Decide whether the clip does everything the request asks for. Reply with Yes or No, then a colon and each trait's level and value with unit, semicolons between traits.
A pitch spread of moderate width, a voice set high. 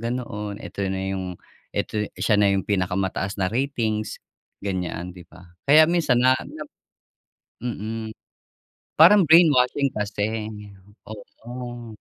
No: average, 4.3 semitones; low, 110 Hz